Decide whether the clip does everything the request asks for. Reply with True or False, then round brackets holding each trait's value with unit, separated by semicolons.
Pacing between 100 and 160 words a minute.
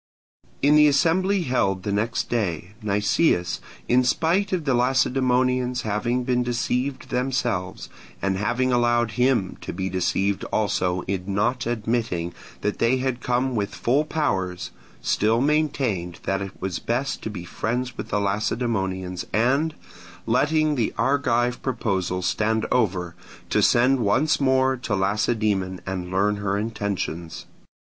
True (135 wpm)